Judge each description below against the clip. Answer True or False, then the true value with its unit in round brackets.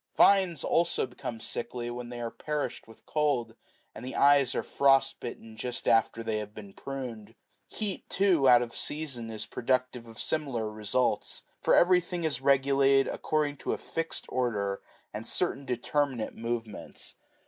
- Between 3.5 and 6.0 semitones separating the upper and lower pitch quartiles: True (3.9 semitones)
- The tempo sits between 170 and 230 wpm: False (155 wpm)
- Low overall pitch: True (125 Hz)